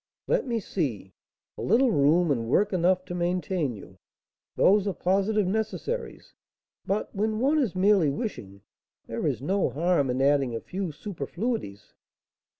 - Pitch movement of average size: No, wide, 6.7 semitones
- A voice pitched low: No, medium, 185 Hz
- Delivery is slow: No, average, 150 wpm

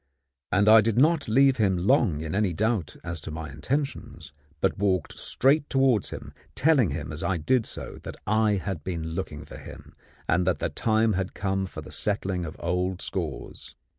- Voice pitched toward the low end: Yes, very low, 95 Hz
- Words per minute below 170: No, average, 190 wpm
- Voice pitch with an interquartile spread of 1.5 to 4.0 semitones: No, average, 4.9 semitones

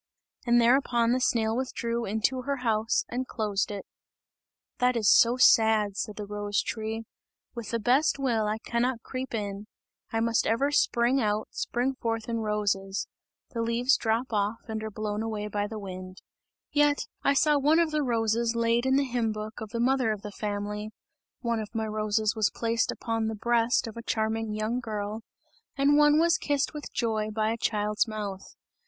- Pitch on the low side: No, high, 225 Hz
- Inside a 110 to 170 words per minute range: No, average, 185 wpm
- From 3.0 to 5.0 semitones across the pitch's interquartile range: No, narrow, 2.4 semitones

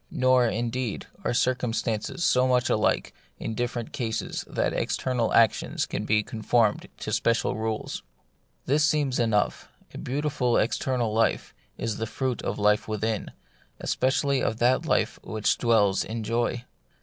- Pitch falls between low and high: No, low, 120 Hz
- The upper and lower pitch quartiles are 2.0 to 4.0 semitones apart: Yes, narrow, 2.5 semitones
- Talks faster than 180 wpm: No, average, 140 wpm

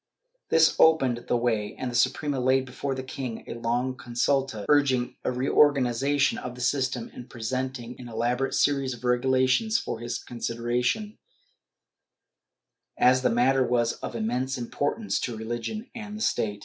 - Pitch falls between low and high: No, low, 125 Hz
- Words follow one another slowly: No, average, 150 wpm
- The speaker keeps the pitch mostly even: Yes, narrow, 2.2 semitones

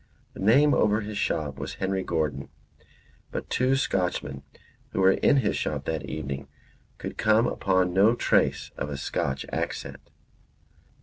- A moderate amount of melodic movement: No, wide, 6.8 semitones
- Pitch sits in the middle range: No, very low, 95 Hz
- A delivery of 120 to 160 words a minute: Yes, average, 145 wpm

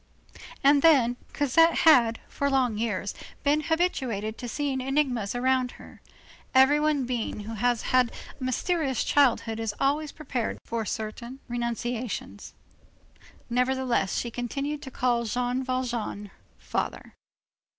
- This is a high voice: Yes, very high, 250 Hz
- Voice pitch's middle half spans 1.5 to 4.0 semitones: Yes, average, 2.9 semitones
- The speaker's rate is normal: No, slow, 120 wpm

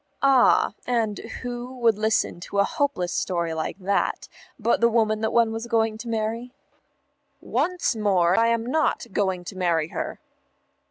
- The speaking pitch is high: Yes, high, 220 Hz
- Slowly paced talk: No, average, 155 wpm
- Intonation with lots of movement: No, average, 3.7 semitones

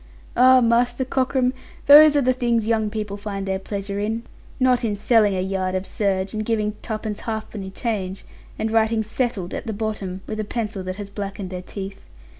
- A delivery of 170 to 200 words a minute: Yes, average, 190 wpm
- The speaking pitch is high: Yes, high, 215 Hz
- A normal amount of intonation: Yes, average, 3.0 semitones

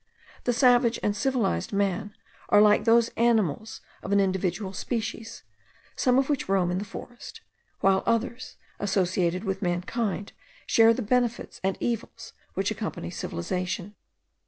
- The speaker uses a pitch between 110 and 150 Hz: No, high, 205 Hz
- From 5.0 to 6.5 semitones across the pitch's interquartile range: No, average, 3.7 semitones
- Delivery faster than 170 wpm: No, slow, 135 wpm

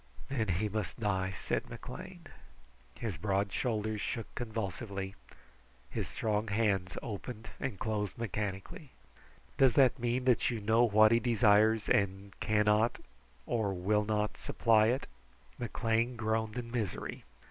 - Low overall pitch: Yes, low, 110 Hz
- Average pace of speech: No, slow, 130 wpm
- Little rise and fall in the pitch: Yes, narrow, 2.3 semitones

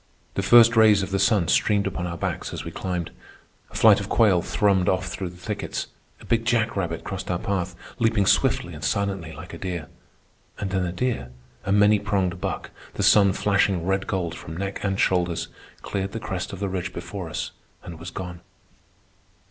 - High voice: No, very low, 95 Hz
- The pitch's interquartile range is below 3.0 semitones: Yes, narrow, 2.4 semitones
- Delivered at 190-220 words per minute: Yes, average, 195 wpm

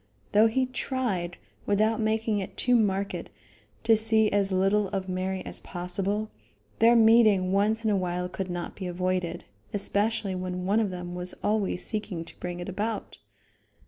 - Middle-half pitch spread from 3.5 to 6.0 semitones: No, average, 3.1 semitones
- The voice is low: No, high, 200 Hz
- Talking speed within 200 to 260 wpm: No, average, 165 wpm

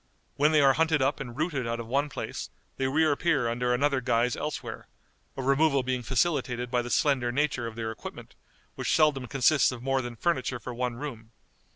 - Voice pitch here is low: Yes, low, 130 Hz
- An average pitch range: Yes, average, 3.2 semitones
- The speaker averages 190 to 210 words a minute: Yes, average, 195 wpm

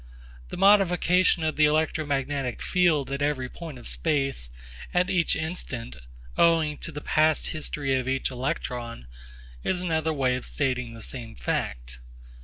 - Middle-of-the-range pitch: Yes, medium, 145 Hz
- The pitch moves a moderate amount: Yes, average, 4.1 semitones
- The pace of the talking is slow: No, average, 145 wpm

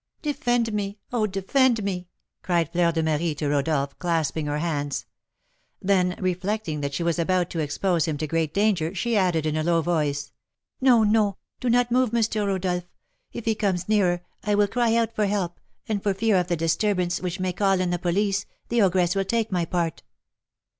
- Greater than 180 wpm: Yes, average, 195 wpm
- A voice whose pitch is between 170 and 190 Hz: Yes, medium, 185 Hz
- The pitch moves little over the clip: No, average, 4.1 semitones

